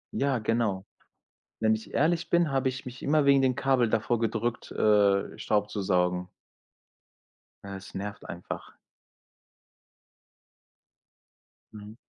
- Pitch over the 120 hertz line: No, low, 110 Hz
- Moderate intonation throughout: Yes, average, 4.6 semitones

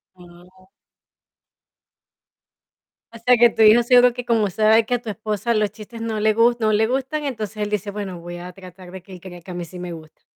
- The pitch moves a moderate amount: Yes, average, 4.0 semitones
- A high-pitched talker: Yes, high, 215 Hz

